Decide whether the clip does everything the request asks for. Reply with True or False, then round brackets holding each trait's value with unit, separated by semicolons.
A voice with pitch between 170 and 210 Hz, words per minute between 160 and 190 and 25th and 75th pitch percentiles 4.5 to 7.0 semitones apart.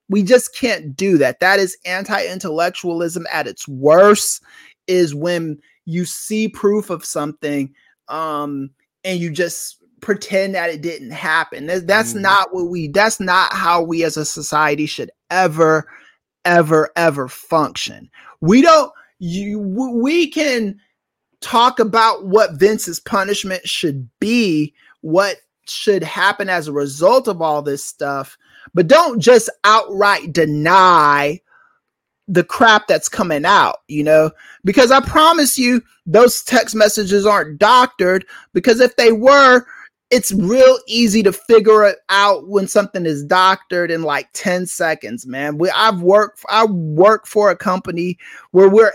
False (190 Hz; 140 wpm; 4.8 semitones)